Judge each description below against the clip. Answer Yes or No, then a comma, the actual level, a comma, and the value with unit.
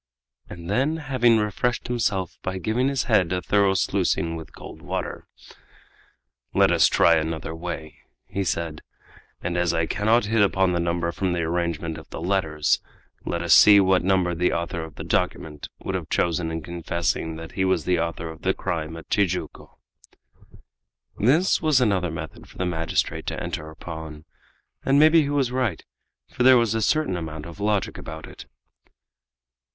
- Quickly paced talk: No, average, 175 wpm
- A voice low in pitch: Yes, very low, 90 Hz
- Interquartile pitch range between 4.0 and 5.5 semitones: Yes, average, 4.5 semitones